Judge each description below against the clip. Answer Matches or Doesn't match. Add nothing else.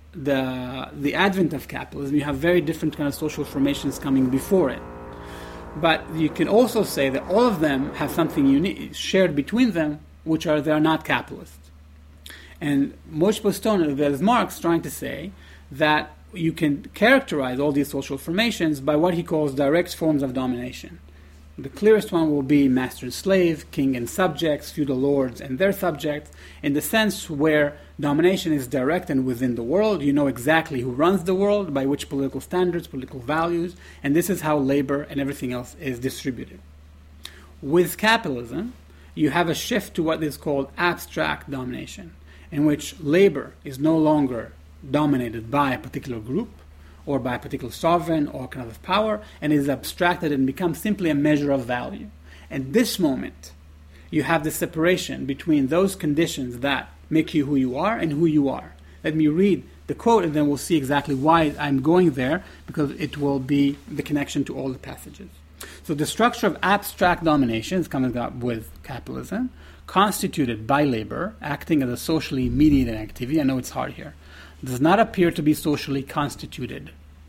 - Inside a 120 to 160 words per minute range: Doesn't match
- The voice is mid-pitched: Matches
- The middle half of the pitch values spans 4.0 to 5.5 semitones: Matches